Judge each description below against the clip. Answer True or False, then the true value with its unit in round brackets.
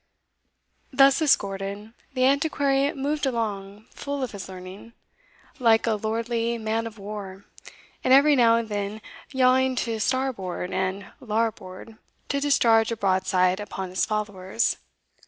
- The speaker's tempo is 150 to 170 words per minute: False (135 wpm)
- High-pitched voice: True (225 Hz)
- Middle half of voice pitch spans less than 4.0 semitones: False (4.7 semitones)